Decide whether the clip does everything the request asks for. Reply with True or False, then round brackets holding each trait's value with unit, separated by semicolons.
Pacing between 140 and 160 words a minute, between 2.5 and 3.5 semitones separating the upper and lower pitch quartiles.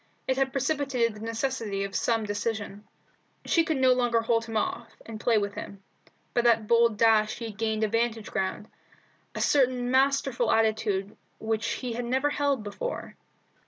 False (170 wpm; 2.9 semitones)